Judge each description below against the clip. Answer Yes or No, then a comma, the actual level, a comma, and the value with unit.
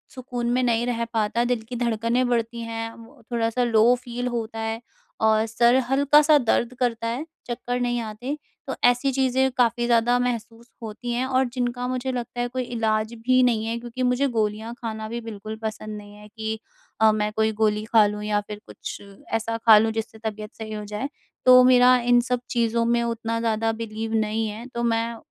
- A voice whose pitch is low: No, high, 230 Hz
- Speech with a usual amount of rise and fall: No, narrow, 1.9 semitones